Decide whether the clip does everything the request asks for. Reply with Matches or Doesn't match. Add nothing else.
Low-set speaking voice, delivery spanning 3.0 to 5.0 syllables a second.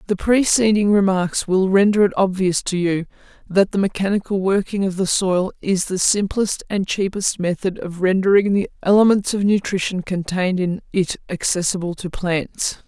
Doesn't match